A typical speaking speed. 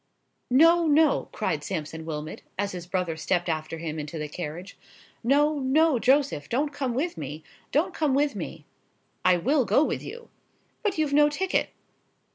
Yes: average, 150 wpm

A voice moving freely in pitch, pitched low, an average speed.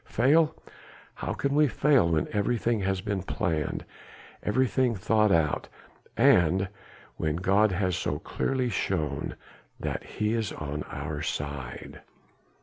No: wide, 6.3 semitones; very low, 95 Hz; slow, 125 wpm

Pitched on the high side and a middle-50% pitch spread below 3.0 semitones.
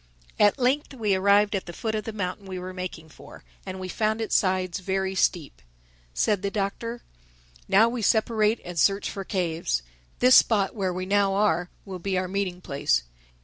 Yes: high, 195 Hz; narrow, 2.6 semitones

